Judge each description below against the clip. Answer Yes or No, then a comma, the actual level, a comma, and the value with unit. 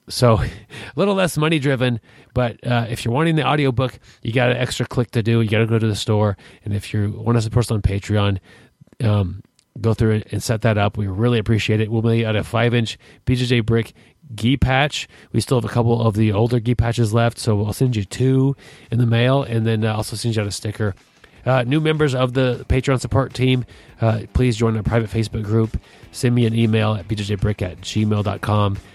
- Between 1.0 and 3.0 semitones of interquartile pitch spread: Yes, narrow, 2.6 semitones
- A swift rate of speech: Yes, fast, 230 wpm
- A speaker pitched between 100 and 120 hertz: Yes, low, 115 Hz